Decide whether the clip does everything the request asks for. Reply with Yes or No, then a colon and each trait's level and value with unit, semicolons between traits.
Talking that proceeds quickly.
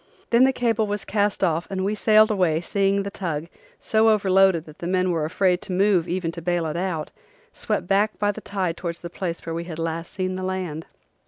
Yes: fast, 225 wpm